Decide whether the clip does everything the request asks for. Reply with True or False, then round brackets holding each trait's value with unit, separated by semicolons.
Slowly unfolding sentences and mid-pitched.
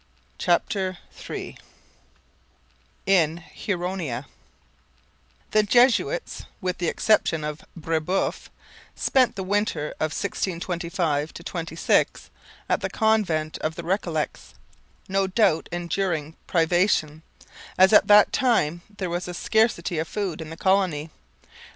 True (110 wpm; 175 Hz)